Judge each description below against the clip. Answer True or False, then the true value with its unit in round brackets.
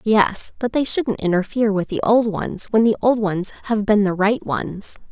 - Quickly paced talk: True (210 wpm)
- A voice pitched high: True (210 Hz)